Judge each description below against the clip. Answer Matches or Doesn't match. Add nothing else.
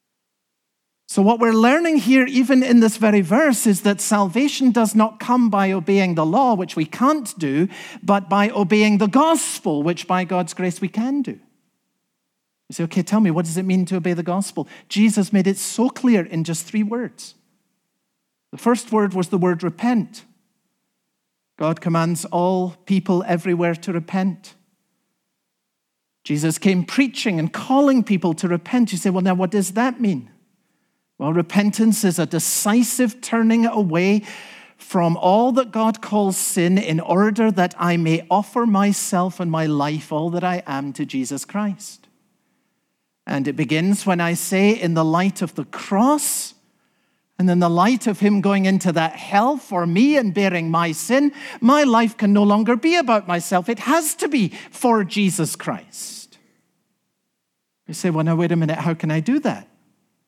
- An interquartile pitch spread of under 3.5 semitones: Doesn't match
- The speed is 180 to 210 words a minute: Doesn't match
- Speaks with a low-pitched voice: Doesn't match